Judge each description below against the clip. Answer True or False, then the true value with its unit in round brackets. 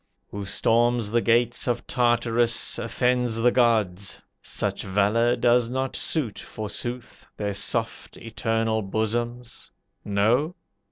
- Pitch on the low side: True (115 Hz)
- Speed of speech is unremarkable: False (110 wpm)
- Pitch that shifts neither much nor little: False (1.8 semitones)